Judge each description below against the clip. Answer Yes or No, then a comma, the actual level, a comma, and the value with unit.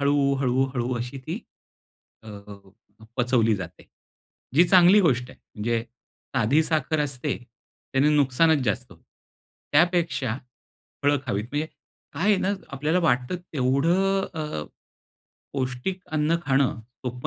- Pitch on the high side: No, medium, 140 Hz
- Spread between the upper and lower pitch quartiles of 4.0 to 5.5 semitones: Yes, average, 4.3 semitones